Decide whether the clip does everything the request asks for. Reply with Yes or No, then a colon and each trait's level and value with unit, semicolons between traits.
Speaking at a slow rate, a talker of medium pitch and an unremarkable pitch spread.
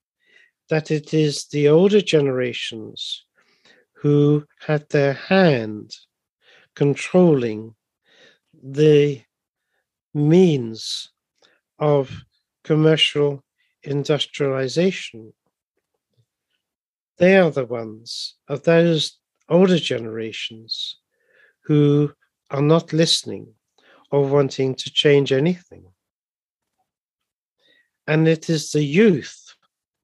Yes: slow, 75 wpm; medium, 145 Hz; average, 3.7 semitones